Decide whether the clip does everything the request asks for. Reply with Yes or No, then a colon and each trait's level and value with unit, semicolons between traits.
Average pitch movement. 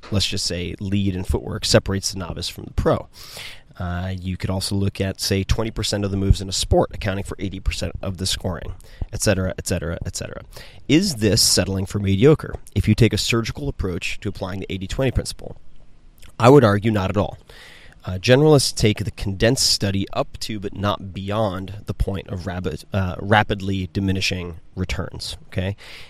No: narrow, 2.3 semitones